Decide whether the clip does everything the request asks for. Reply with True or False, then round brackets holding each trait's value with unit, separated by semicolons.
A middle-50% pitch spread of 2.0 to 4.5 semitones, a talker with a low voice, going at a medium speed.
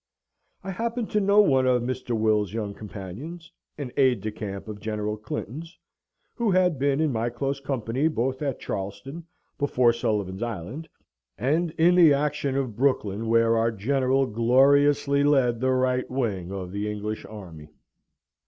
False (4.9 semitones; 125 Hz; 155 wpm)